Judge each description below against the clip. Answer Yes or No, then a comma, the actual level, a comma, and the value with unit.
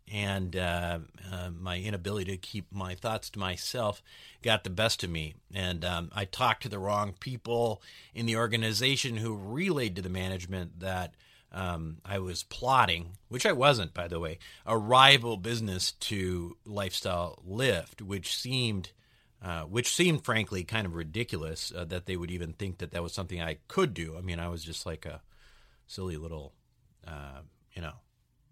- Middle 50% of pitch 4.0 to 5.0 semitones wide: Yes, average, 4.4 semitones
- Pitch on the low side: Yes, very low, 95 Hz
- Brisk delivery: No, average, 175 wpm